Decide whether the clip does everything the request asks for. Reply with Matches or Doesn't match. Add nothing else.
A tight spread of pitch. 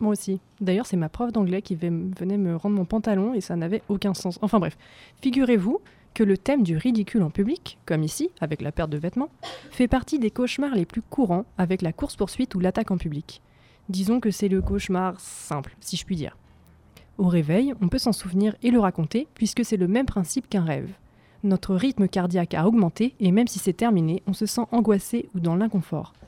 Doesn't match